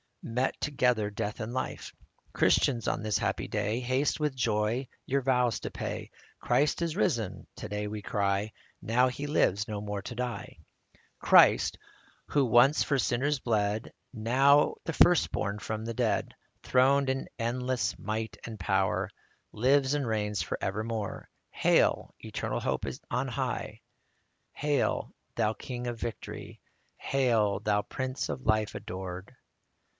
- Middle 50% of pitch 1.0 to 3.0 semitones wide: No, average, 3.8 semitones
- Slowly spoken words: No, average, 145 wpm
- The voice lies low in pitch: Yes, low, 115 Hz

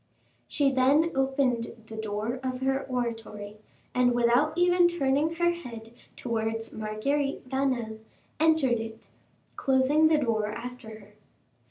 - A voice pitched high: Yes, very high, 255 Hz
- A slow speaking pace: Yes, slow, 125 wpm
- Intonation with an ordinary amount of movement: Yes, average, 4.0 semitones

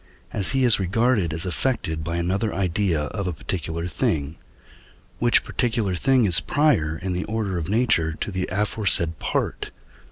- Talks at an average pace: Yes, average, 165 wpm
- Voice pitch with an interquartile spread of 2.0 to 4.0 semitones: No, average, 5.0 semitones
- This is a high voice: No, very low, 95 Hz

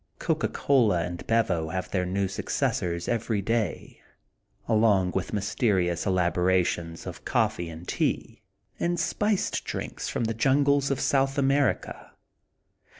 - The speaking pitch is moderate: No, low, 100 Hz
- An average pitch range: No, wide, 6.6 semitones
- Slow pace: Yes, slow, 125 wpm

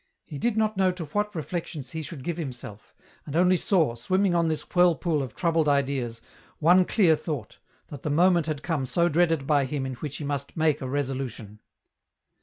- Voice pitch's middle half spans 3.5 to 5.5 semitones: Yes, average, 4.2 semitones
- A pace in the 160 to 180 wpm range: No, average, 195 wpm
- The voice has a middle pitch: Yes, medium, 155 Hz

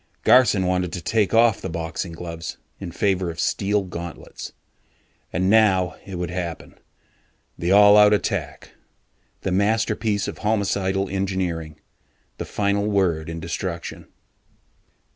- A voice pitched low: Yes, very low, 95 Hz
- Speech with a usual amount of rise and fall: Yes, average, 3.1 semitones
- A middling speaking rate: No, slow, 125 wpm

